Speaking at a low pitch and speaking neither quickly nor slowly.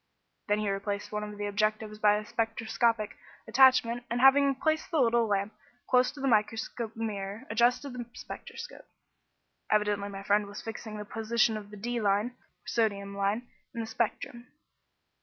No: high, 220 Hz; average, 165 wpm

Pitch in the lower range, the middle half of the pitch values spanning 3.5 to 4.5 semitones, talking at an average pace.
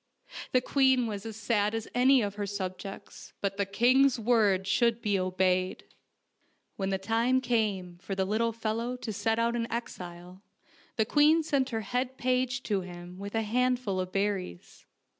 No: high, 220 Hz; average, 4.1 semitones; average, 170 wpm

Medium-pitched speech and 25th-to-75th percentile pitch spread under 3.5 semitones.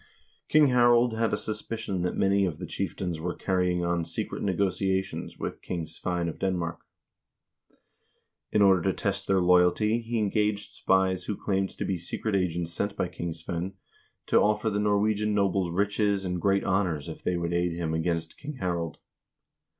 No: very low, 95 Hz; average, 2.8 semitones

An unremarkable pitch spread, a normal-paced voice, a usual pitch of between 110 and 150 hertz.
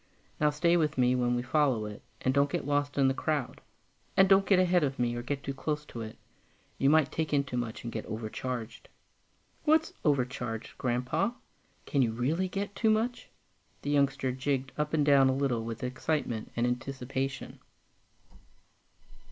Yes: average, 3.5 semitones; average, 175 wpm; low, 135 Hz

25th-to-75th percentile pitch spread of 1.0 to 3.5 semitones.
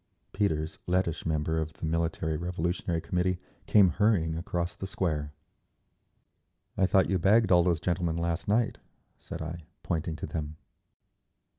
Yes: narrow, 2.6 semitones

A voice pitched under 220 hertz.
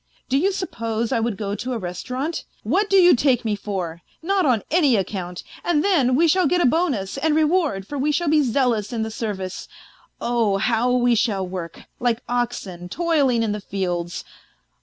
No: high, 240 Hz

